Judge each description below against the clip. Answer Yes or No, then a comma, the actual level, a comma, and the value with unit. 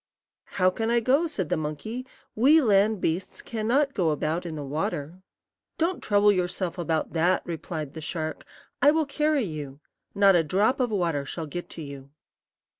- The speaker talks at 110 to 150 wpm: No, average, 180 wpm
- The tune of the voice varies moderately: No, wide, 6.5 semitones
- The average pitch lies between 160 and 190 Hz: Yes, medium, 185 Hz